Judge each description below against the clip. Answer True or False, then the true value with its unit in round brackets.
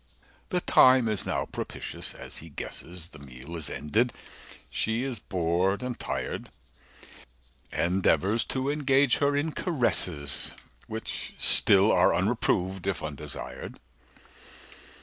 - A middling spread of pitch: False (7.0 semitones)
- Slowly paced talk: True (120 wpm)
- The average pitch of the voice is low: True (100 Hz)